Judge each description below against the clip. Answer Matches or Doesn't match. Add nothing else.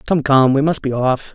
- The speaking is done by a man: Matches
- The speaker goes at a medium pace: Doesn't match